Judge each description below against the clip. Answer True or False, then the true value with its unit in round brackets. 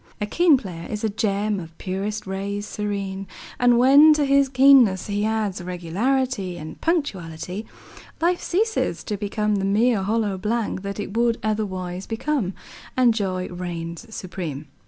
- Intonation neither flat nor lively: True (4.2 semitones)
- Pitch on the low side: False (205 Hz)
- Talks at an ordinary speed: True (150 wpm)